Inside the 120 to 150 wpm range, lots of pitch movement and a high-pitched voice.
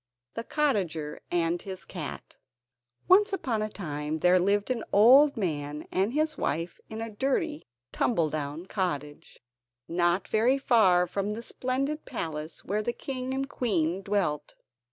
Yes: average, 145 wpm; wide, 7.2 semitones; high, 200 Hz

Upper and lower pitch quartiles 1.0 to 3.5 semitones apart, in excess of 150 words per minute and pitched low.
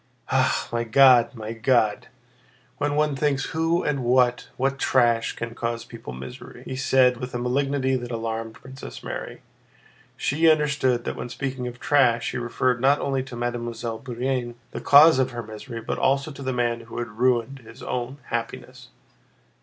Yes: narrow, 2.5 semitones; average, 165 wpm; low, 125 Hz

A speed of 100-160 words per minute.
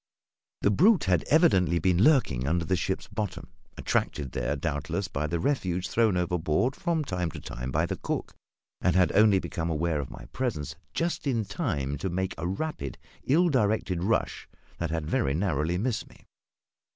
No: average, 175 wpm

